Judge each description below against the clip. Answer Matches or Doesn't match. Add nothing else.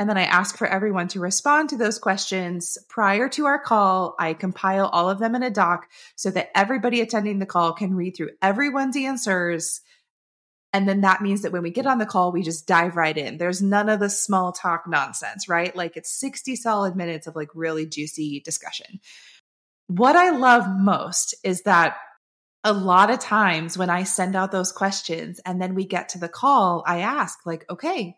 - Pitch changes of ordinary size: Matches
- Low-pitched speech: Doesn't match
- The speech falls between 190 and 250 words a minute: Matches